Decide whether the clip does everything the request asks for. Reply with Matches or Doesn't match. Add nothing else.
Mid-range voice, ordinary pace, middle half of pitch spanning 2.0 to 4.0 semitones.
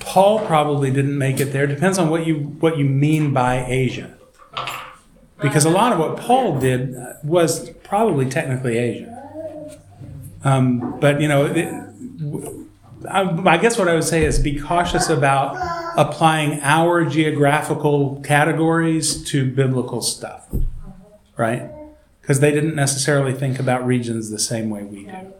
Matches